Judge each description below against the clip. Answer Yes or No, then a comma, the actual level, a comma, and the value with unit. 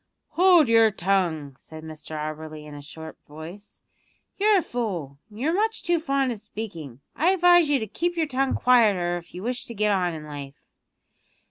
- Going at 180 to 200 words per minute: Yes, average, 190 wpm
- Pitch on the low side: No, high, 210 Hz